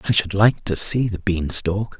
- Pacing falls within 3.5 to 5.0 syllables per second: Yes, 4.4 syllables/s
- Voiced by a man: Yes, male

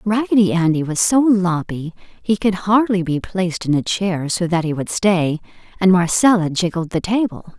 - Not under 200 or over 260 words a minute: No, average, 180 wpm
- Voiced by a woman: Yes, female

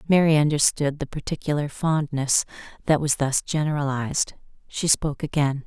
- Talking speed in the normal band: No, slow, 125 wpm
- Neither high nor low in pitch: Yes, medium, 145 Hz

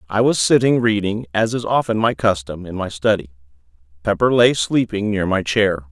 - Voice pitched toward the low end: Yes, low, 100 Hz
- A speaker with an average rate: Yes, average, 185 wpm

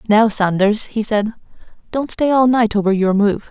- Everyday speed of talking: Yes, average, 190 wpm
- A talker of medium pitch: No, high, 215 Hz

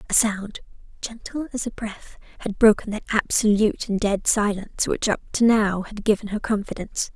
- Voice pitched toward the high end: Yes, high, 210 Hz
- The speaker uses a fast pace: No, average, 160 wpm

